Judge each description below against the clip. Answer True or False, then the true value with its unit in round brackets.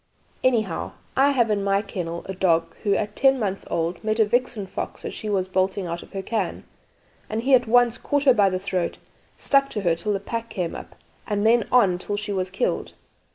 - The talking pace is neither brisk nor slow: False (220 wpm)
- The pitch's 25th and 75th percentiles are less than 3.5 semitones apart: False (3.8 semitones)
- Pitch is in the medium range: False (205 Hz)